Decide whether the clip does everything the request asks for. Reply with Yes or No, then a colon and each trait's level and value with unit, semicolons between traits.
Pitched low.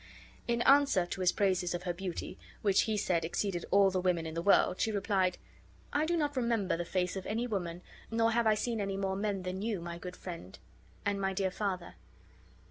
No: high, 195 Hz